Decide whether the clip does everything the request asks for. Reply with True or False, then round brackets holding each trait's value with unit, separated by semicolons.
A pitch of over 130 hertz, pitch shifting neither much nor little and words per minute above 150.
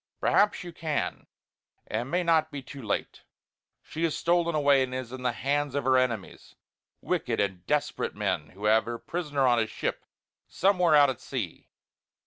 True (140 Hz; 4.8 semitones; 180 wpm)